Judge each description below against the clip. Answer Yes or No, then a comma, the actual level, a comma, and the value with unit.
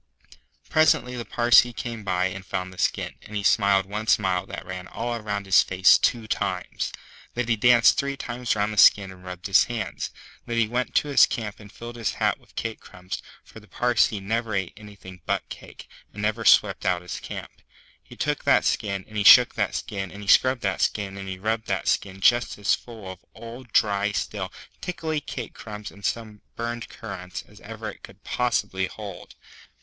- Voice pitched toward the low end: Yes, low, 105 Hz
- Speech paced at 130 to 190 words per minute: No, average, 200 wpm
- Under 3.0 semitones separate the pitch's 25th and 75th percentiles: No, average, 3.3 semitones